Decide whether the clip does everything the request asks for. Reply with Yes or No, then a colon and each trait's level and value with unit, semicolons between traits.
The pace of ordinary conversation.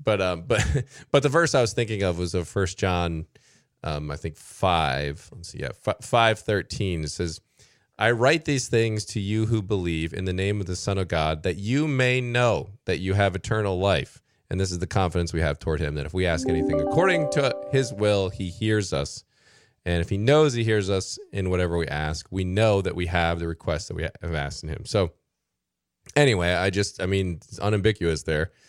No: fast, 220 wpm